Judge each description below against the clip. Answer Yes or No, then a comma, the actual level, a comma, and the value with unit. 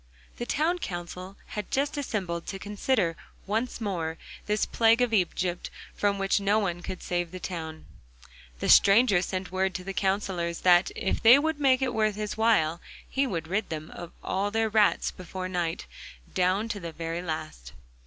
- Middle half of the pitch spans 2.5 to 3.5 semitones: No, average, 3.9 semitones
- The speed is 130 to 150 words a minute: No, average, 175 wpm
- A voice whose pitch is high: Yes, high, 195 Hz